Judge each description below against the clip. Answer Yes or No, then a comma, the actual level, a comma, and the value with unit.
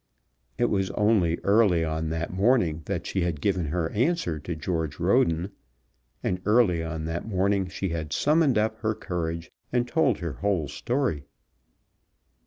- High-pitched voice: No, very low, 90 Hz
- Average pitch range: Yes, average, 4.9 semitones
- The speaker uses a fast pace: No, average, 155 wpm